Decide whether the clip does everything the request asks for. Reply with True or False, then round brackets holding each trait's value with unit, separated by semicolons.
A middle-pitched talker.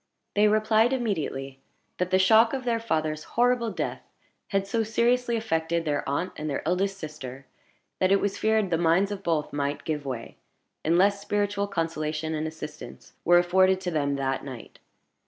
True (180 Hz)